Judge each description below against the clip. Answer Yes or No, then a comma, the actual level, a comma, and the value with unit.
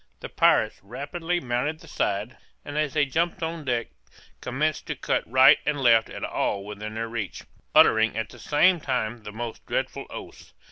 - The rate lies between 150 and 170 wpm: No, average, 180 wpm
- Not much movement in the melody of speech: No, average, 5.3 semitones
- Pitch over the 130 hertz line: No, low, 125 Hz